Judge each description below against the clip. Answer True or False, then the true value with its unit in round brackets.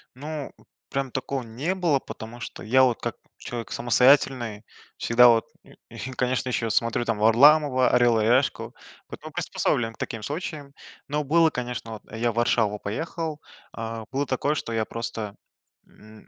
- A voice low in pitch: True (125 Hz)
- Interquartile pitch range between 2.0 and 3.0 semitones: False (3.5 semitones)